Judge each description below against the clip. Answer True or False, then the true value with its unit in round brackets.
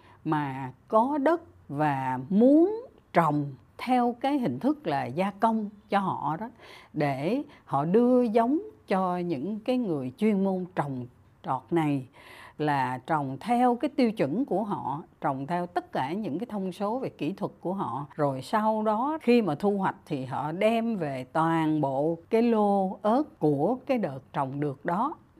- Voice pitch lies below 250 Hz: True (185 Hz)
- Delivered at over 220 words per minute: False (170 wpm)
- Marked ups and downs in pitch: True (8.1 semitones)